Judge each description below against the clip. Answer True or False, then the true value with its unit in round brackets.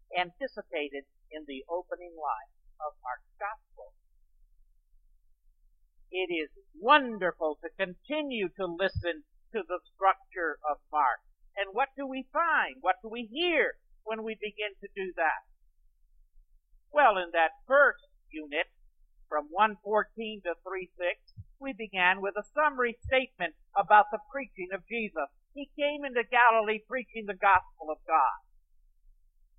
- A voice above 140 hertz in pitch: True (185 Hz)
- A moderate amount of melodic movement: False (8.4 semitones)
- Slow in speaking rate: True (130 wpm)